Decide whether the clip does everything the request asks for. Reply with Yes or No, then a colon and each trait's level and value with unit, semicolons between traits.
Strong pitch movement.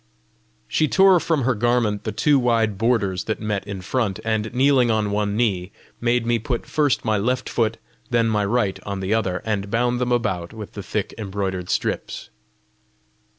No: average, 3.3 semitones